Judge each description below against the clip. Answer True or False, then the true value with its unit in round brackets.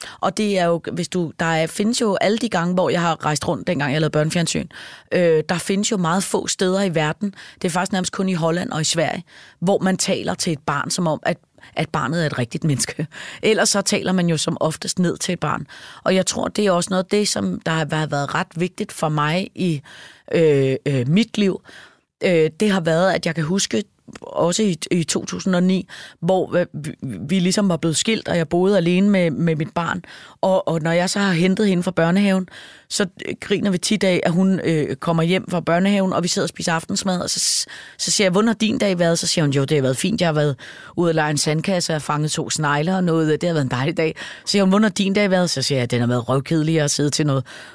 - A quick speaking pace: True (250 wpm)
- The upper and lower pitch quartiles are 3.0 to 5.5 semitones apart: True (3.3 semitones)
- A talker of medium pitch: True (175 Hz)